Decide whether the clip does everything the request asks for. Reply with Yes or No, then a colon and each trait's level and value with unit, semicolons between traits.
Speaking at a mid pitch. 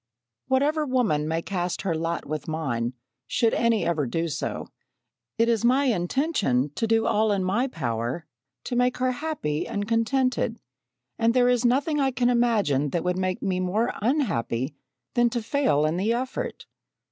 No: high, 220 Hz